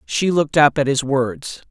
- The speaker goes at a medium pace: No, fast, 210 wpm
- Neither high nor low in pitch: Yes, medium, 145 Hz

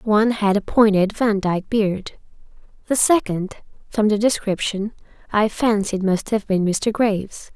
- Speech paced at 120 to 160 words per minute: Yes, average, 145 wpm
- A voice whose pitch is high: Yes, high, 205 Hz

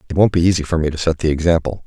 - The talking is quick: Yes, fast, 320 wpm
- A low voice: Yes, very low, 80 Hz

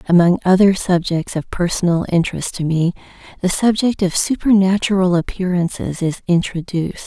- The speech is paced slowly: Yes, slow, 125 wpm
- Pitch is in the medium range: Yes, medium, 180 Hz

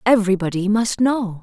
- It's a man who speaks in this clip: No, female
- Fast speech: No, slow, 125 wpm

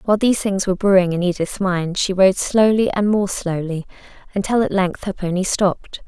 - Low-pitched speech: No, high, 190 Hz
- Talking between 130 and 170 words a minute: No, average, 200 wpm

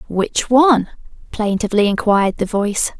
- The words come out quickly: No, slow, 120 wpm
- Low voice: No, high, 215 Hz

